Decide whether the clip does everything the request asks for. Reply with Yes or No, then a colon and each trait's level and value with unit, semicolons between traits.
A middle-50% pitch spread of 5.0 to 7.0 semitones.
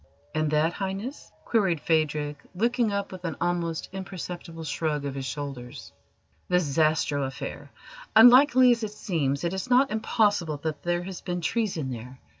Yes: average, 5.3 semitones